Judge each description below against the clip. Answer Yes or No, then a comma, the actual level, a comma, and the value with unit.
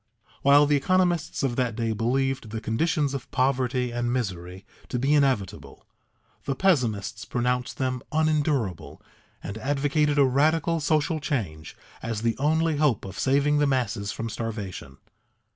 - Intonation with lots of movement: No, average, 4.4 semitones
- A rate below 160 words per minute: Yes, average, 145 wpm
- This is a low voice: Yes, low, 130 Hz